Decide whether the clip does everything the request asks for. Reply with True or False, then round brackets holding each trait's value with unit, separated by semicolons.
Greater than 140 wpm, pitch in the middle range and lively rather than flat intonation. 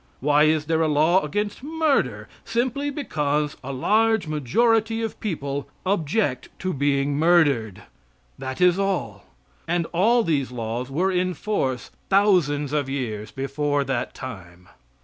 False (135 wpm; 150 Hz; 6.3 semitones)